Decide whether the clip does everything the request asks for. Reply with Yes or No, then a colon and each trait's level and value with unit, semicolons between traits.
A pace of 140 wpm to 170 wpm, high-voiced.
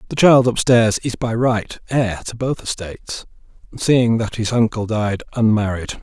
No: average, 160 wpm; low, 115 Hz